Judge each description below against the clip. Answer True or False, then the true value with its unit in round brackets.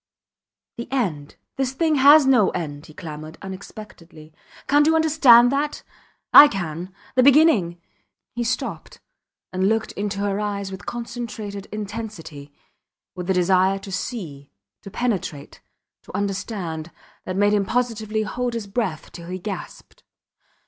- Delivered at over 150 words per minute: False (135 wpm)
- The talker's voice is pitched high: True (205 Hz)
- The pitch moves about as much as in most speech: True (4.9 semitones)